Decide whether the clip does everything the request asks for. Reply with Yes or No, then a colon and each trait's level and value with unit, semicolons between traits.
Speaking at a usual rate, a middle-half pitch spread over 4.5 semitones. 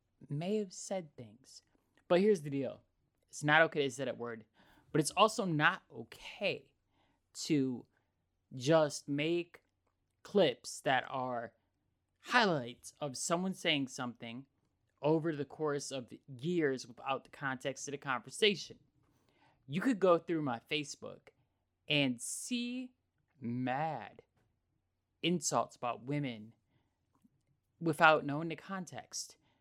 No: slow, 120 wpm; average, 5.2 semitones